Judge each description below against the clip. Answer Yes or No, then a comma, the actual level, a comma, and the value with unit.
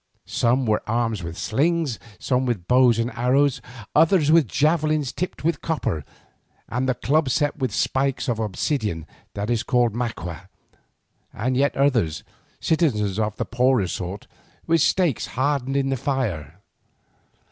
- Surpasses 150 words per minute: No, average, 145 wpm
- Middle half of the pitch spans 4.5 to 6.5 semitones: Yes, average, 4.8 semitones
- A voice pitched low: Yes, low, 125 Hz